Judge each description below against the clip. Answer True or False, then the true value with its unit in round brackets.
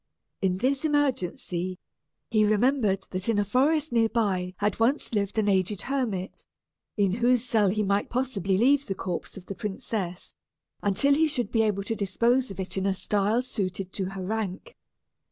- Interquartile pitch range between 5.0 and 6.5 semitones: False (4.3 semitones)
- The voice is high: True (210 Hz)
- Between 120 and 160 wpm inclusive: False (175 wpm)